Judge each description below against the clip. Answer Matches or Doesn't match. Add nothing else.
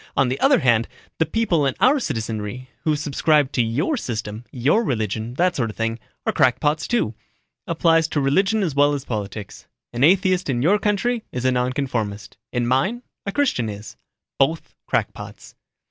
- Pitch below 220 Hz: Matches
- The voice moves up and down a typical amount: Doesn't match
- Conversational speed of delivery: Matches